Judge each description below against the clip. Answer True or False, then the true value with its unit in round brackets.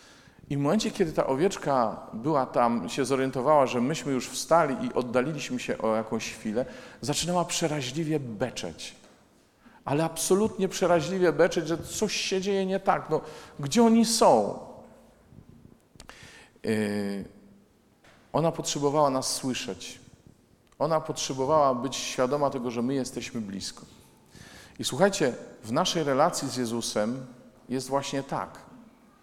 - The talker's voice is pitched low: False (145 Hz)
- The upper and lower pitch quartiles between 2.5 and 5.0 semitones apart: False (5.4 semitones)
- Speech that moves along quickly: False (125 wpm)